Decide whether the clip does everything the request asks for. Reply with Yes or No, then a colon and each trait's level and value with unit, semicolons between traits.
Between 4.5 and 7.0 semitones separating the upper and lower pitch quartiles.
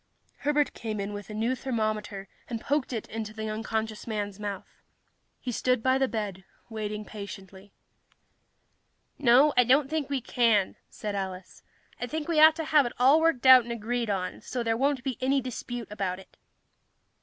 No: average, 3.8 semitones